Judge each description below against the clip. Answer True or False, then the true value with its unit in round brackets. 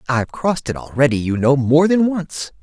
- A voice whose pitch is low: False (145 Hz)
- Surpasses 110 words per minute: True (205 wpm)